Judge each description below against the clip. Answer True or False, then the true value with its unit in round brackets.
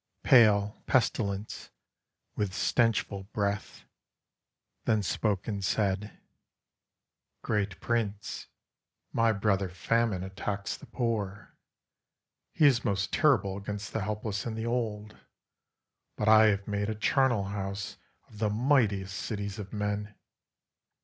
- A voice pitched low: True (105 Hz)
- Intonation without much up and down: True (2.0 semitones)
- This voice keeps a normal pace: False (115 wpm)